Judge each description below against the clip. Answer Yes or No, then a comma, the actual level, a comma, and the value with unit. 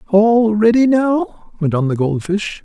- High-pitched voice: Yes, high, 205 Hz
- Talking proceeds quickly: No, average, 180 wpm